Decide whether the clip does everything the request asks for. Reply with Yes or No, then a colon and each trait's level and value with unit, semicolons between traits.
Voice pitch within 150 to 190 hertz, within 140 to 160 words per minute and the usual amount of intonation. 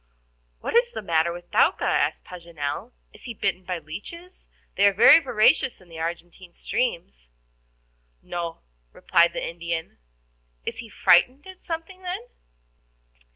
No: medium, 185 Hz; average, 145 wpm; wide, 8.4 semitones